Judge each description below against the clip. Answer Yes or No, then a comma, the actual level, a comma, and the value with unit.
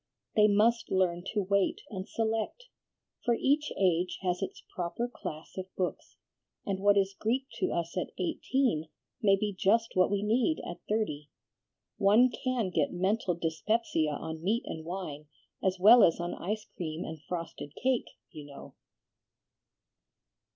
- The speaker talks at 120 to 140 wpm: No, average, 150 wpm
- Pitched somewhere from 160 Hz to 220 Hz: Yes, high, 190 Hz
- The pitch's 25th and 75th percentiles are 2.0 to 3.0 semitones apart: No, average, 4.5 semitones